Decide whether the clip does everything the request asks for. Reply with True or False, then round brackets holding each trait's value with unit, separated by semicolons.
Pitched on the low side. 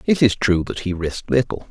True (105 Hz)